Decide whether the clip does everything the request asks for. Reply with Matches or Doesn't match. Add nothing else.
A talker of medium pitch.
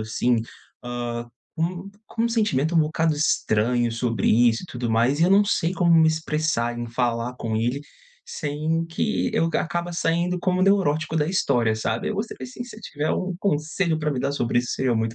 Matches